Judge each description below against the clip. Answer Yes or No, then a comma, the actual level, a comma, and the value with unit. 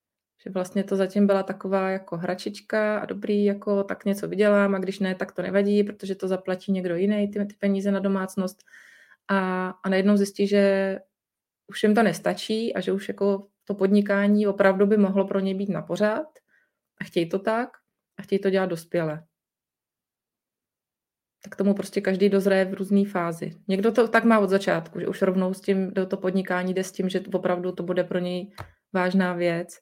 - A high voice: Yes, high, 195 Hz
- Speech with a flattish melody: Yes, narrow, 1.2 semitones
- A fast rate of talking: Yes, fast, 195 wpm